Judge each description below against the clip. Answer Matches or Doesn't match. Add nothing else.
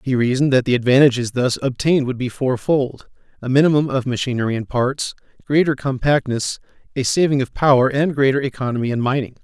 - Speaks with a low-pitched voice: Matches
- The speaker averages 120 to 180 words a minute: Matches